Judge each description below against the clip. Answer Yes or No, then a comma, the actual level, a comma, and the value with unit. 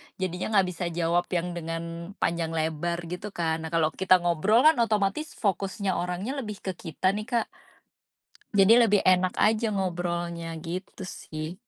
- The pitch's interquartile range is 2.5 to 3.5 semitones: Yes, average, 3.1 semitones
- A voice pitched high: No, medium, 180 Hz